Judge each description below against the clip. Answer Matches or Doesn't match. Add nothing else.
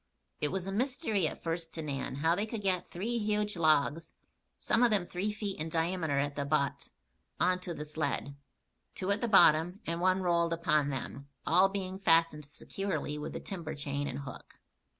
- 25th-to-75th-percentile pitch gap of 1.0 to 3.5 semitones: Doesn't match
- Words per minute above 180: Matches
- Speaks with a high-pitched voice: Doesn't match